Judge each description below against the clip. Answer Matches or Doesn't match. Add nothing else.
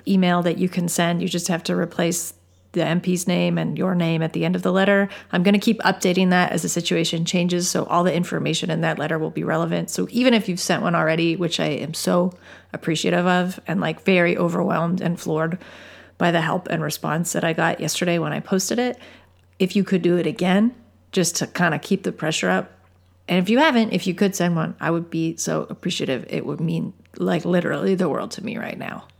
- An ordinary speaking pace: Doesn't match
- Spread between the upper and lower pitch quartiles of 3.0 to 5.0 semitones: Doesn't match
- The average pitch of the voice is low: Doesn't match